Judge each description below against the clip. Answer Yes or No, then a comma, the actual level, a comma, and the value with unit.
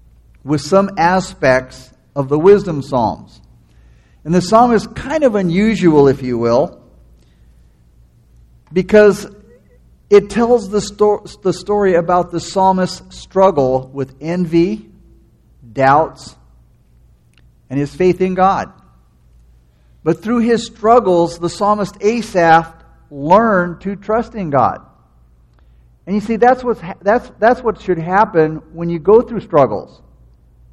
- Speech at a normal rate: No, slow, 125 wpm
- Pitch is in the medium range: Yes, medium, 170 Hz